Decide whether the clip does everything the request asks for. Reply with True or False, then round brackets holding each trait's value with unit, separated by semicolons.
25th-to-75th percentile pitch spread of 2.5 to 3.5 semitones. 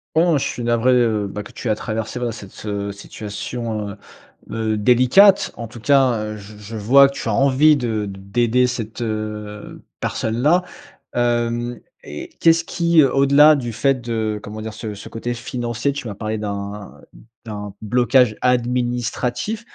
True (2.9 semitones)